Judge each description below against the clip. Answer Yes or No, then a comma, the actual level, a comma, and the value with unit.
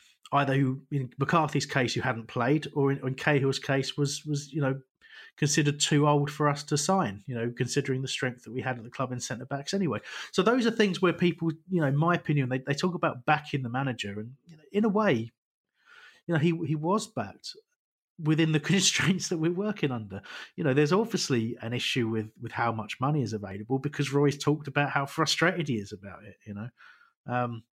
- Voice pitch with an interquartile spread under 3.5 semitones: No, average, 4.3 semitones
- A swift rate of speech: Yes, fast, 220 wpm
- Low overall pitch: No, medium, 145 Hz